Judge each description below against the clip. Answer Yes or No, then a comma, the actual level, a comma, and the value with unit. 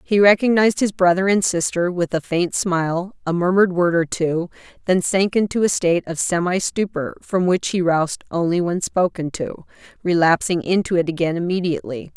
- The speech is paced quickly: No, average, 180 wpm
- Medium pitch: Yes, medium, 175 Hz